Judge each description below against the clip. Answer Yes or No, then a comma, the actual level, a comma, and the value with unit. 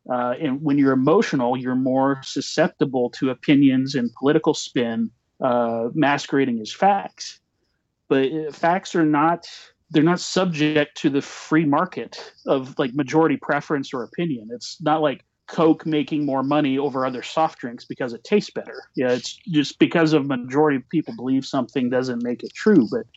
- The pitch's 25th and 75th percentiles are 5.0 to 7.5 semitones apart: No, average, 3.3 semitones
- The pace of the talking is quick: No, average, 165 wpm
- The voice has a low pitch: No, medium, 145 Hz